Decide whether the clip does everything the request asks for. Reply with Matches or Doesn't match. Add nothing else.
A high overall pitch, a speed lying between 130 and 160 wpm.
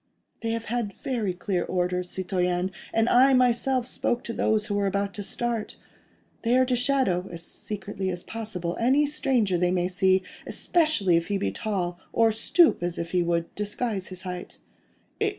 Doesn't match